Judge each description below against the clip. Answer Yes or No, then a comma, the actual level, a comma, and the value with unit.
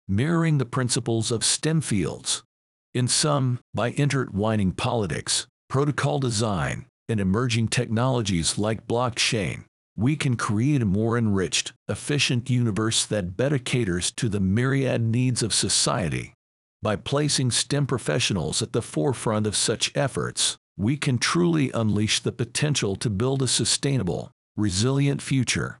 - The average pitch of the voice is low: Yes, low, 120 Hz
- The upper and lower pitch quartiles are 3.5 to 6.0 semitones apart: Yes, average, 4.0 semitones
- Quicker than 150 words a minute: No, slow, 135 wpm